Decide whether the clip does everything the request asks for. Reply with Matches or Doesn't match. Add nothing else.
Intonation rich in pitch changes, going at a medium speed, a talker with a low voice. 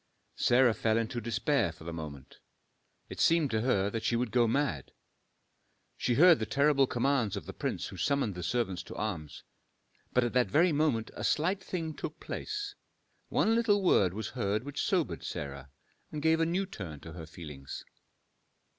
Matches